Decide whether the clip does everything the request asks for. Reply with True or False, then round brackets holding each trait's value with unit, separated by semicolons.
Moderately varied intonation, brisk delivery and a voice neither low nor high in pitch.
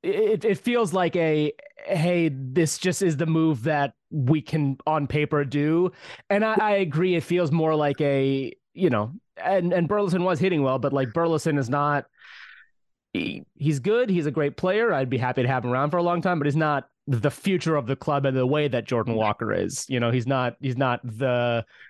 True (4.6 semitones; 215 wpm; 150 Hz)